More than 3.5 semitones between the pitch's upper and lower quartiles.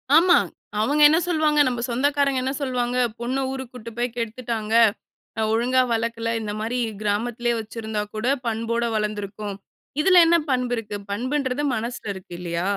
No: average, 3.1 semitones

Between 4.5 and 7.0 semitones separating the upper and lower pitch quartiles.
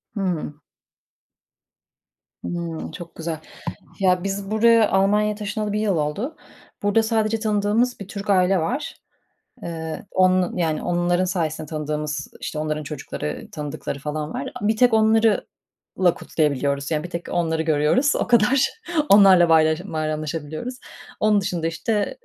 Yes: average, 5.2 semitones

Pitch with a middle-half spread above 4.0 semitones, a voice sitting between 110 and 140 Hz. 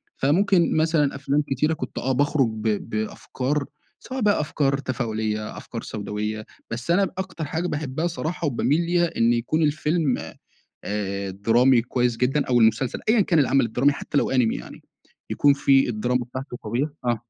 Yes: average, 4.8 semitones; low, 135 Hz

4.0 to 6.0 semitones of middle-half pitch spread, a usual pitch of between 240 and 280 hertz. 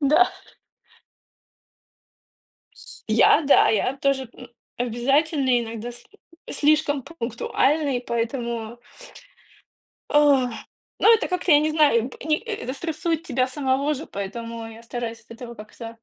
Yes: average, 4.3 semitones; very high, 260 Hz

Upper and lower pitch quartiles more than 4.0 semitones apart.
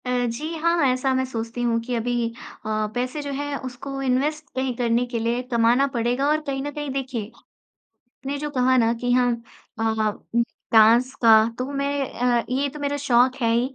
No: average, 2.7 semitones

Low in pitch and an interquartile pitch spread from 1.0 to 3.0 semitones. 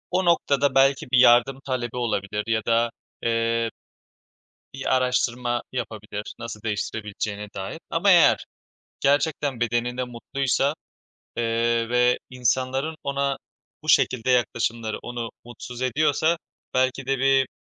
Yes: low, 125 Hz; average, 2.7 semitones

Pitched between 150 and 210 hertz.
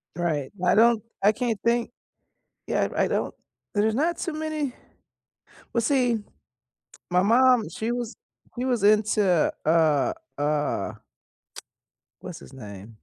No: high, 220 Hz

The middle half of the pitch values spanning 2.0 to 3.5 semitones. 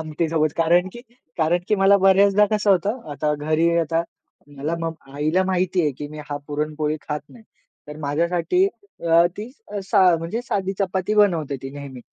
No: average, 4.1 semitones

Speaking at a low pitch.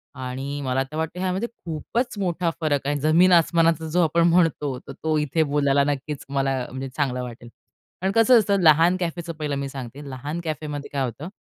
No: medium, 155 Hz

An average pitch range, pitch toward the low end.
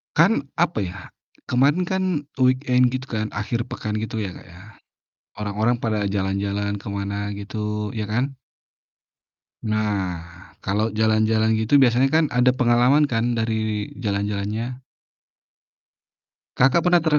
Yes: average, 3.7 semitones; low, 110 Hz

